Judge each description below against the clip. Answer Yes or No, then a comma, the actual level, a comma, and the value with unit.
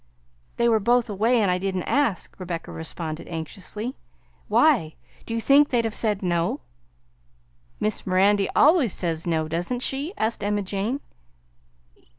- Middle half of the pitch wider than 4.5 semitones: Yes, average, 5.2 semitones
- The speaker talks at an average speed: Yes, average, 145 wpm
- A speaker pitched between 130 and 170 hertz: No, high, 205 Hz